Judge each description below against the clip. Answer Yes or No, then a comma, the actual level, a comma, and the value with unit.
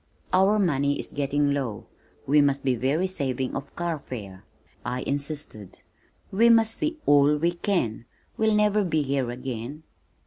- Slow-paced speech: No, average, 145 wpm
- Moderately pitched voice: Yes, medium, 145 Hz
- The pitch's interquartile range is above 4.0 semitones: Yes, wide, 5.5 semitones